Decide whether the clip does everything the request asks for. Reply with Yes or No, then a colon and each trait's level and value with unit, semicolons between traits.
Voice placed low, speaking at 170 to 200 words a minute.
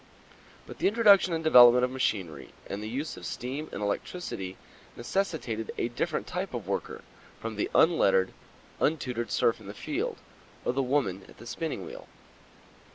No: low, 125 Hz; average, 160 wpm